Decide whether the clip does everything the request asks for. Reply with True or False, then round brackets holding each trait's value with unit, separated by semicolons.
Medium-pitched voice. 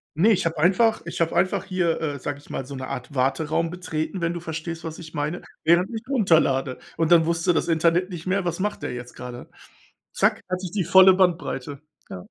True (165 Hz)